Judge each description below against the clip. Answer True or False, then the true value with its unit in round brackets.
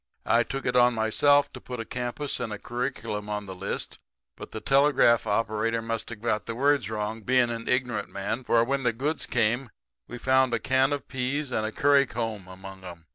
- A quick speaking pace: True (210 wpm)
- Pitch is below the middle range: True (120 Hz)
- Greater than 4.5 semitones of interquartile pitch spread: False (3.2 semitones)